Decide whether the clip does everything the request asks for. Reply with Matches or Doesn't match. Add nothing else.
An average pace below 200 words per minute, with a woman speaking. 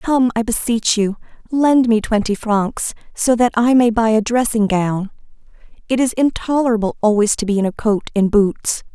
Matches